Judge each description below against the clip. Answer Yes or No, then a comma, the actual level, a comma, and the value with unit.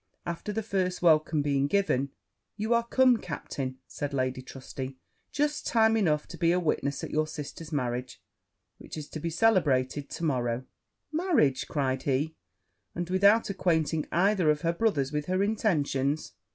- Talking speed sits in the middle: Yes, average, 160 wpm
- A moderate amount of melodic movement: No, wide, 6.1 semitones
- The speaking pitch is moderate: Yes, medium, 155 Hz